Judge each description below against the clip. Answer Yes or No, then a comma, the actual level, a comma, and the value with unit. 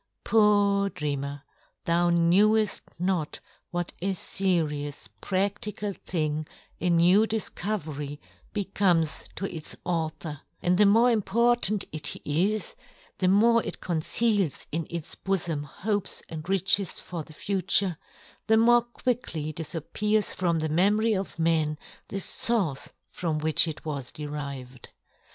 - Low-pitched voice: No, medium, 180 Hz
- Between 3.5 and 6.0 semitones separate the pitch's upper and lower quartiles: Yes, average, 4.7 semitones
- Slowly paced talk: Yes, slow, 130 wpm